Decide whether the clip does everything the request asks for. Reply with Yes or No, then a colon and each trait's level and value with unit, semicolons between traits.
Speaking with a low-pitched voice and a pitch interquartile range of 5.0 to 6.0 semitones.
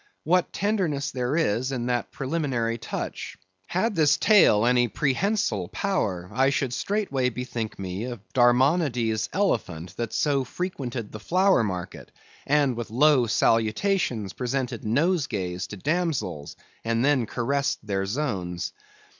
Yes: low, 125 Hz; wide, 5.4 semitones